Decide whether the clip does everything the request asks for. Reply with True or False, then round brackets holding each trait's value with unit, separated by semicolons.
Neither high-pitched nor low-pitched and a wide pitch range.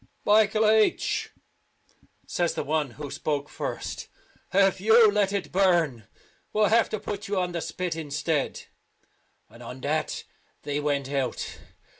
True (175 Hz; 6.0 semitones)